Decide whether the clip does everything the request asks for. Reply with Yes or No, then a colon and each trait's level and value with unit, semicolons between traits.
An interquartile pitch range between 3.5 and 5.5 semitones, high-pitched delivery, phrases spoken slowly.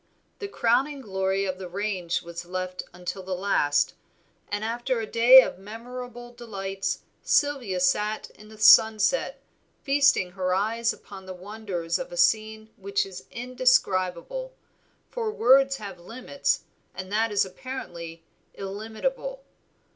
Yes: average, 4.8 semitones; high, 210 Hz; slow, 130 wpm